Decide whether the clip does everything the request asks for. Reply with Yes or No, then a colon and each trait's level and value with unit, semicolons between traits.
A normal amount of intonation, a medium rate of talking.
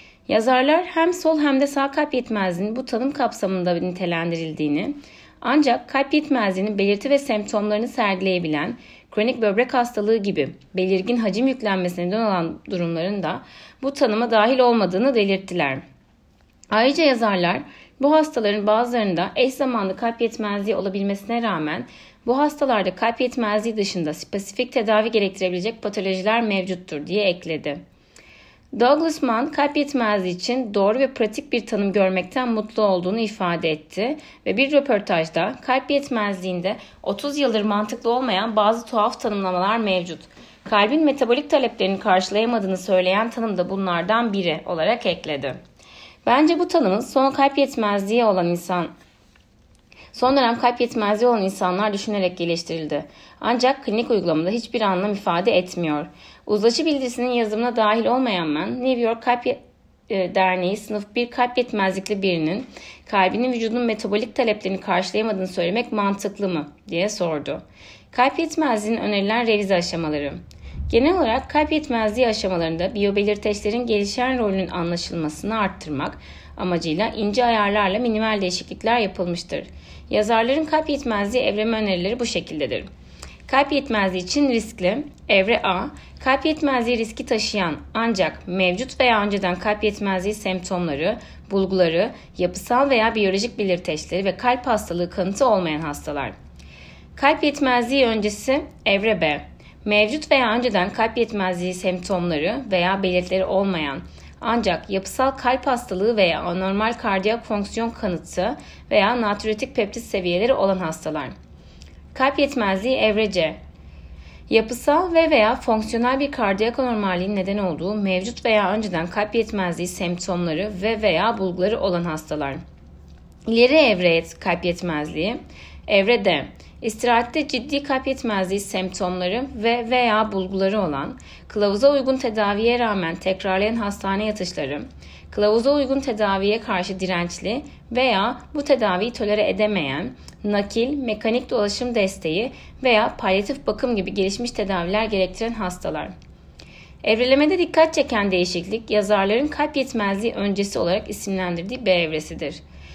Yes: average, 4.7 semitones; average, 120 wpm